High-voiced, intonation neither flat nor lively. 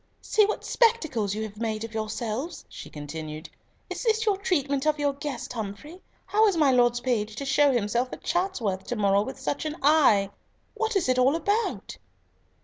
No: very high, 260 Hz; wide, 7.4 semitones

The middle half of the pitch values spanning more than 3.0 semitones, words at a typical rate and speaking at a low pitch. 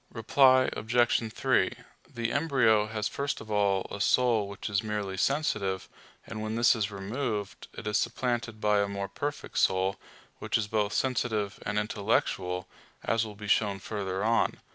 No: narrow, 2.6 semitones; average, 165 wpm; low, 110 Hz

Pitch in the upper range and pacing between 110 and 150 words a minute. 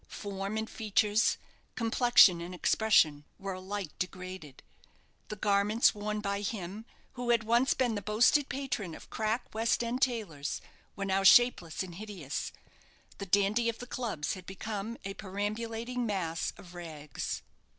Yes: high, 205 Hz; average, 145 wpm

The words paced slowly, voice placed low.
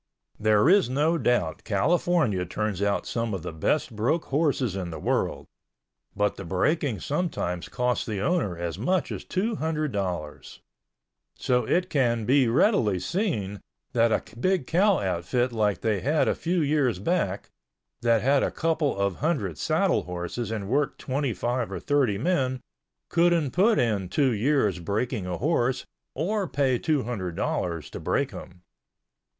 No: average, 155 wpm; low, 120 Hz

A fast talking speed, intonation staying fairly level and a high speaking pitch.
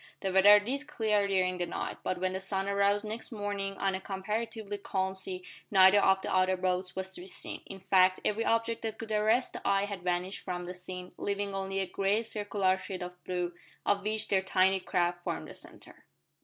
Yes: fast, 210 wpm; narrow, 1.8 semitones; high, 195 Hz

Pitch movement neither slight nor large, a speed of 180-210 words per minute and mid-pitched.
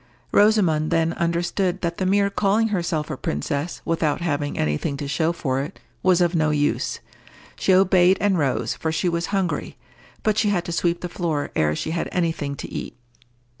Yes: average, 3.5 semitones; average, 195 wpm; medium, 170 Hz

